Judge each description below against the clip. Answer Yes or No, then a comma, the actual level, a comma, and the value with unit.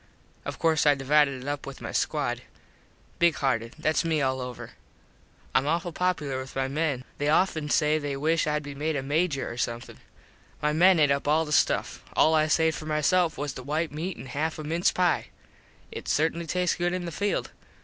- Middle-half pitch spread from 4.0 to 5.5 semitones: No, average, 2.8 semitones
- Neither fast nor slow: No, fast, 210 wpm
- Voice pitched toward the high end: No, medium, 150 Hz